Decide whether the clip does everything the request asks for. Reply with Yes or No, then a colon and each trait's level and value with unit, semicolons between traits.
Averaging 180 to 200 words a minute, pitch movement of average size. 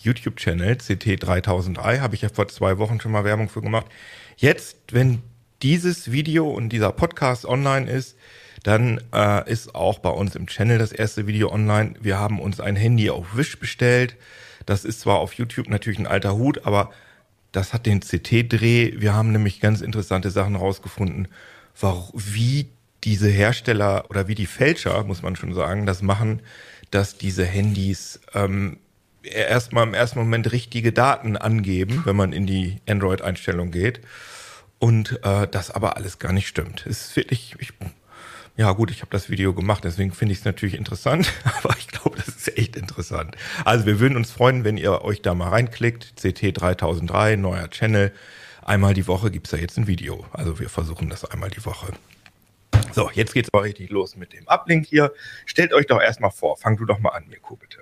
Yes: average, 185 wpm; average, 3.1 semitones